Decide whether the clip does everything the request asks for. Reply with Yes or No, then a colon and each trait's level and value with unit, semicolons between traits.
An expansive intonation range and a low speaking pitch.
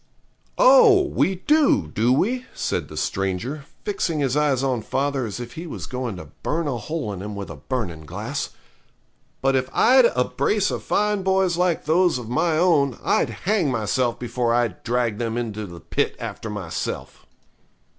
Yes: wide, 7.6 semitones; low, 130 Hz